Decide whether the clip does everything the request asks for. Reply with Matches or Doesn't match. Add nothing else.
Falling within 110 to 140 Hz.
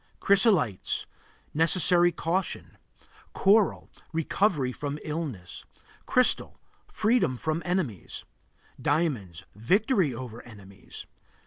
Doesn't match